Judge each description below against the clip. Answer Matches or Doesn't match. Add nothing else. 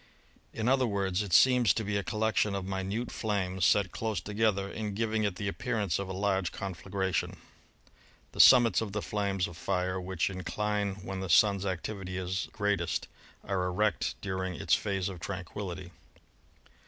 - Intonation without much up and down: Matches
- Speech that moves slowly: Doesn't match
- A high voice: Doesn't match